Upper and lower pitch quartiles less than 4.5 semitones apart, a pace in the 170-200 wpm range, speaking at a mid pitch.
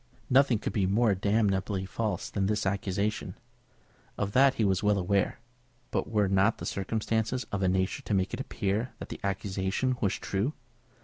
No: narrow, 2.5 semitones; average, 175 wpm; low, 100 Hz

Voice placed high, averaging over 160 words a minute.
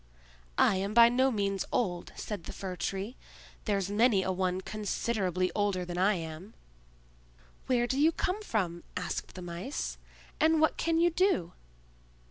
No: high, 200 Hz; average, 155 wpm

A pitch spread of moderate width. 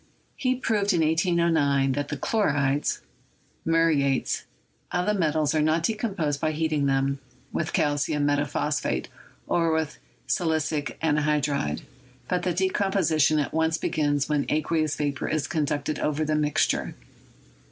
No: narrow, 2.2 semitones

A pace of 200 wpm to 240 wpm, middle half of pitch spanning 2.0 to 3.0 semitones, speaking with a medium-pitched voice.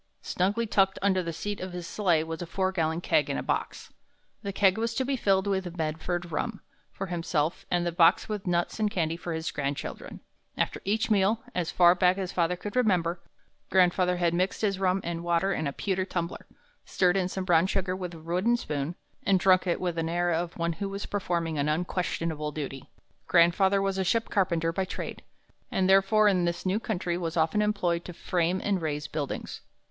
Yes: fast, 205 wpm; narrow, 2.5 semitones; medium, 180 Hz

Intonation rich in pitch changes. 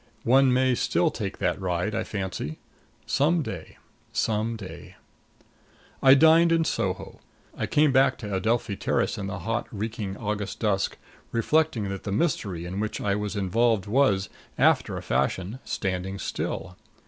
No: average, 4.9 semitones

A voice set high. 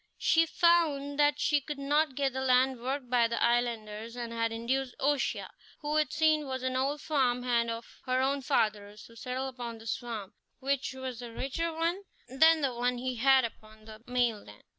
Yes: very high, 255 Hz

